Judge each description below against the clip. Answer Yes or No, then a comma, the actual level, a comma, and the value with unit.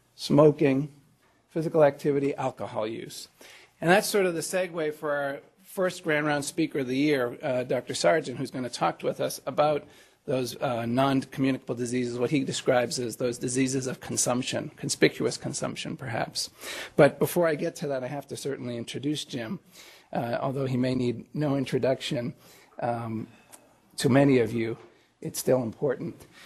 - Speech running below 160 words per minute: No, average, 165 wpm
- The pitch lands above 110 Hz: Yes, medium, 140 Hz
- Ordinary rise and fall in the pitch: Yes, average, 3.0 semitones